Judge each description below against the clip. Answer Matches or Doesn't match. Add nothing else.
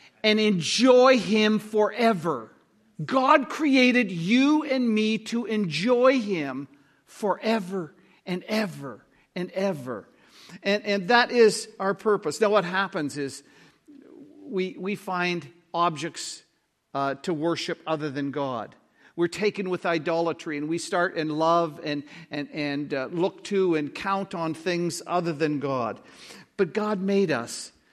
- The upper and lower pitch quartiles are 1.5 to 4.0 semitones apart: Doesn't match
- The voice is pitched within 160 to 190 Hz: Matches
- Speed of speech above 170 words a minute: Doesn't match